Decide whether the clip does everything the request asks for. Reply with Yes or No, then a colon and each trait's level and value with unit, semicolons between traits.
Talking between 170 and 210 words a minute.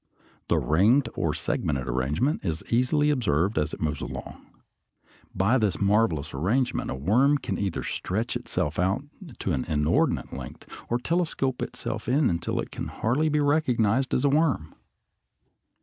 No: average, 150 wpm